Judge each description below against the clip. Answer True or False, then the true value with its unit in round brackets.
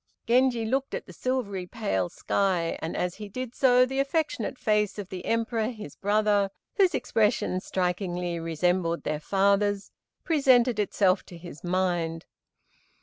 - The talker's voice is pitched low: False (205 Hz)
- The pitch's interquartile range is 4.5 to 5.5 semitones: True (5.0 semitones)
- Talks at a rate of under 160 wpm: True (145 wpm)